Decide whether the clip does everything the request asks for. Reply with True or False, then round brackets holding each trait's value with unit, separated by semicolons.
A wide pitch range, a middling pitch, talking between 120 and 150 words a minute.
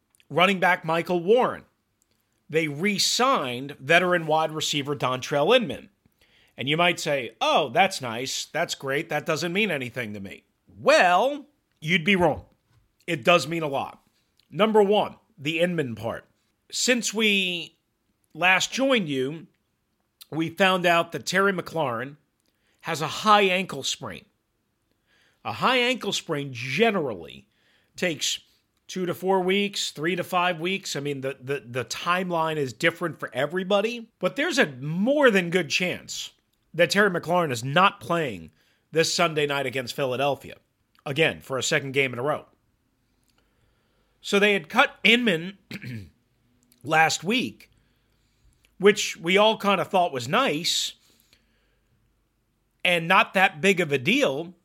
True (6.4 semitones; 165 Hz; 140 wpm)